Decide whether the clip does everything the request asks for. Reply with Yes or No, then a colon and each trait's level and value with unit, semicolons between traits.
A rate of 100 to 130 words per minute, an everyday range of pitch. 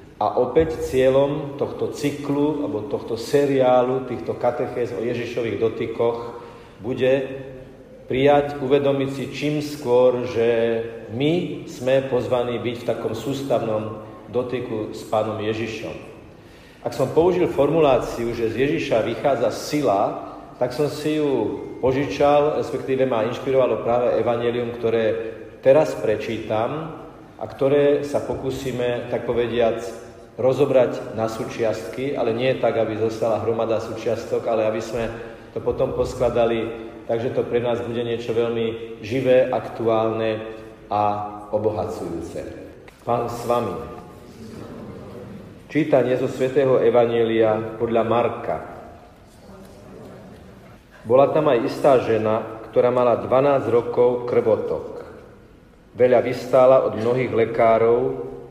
Yes: average, 115 wpm; average, 3.3 semitones